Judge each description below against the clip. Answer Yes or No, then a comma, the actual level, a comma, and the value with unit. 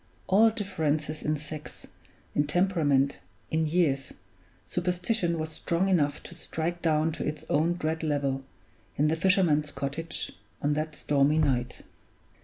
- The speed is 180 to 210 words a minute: No, slow, 135 wpm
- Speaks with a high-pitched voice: No, medium, 155 Hz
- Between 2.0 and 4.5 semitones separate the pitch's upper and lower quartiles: Yes, average, 2.9 semitones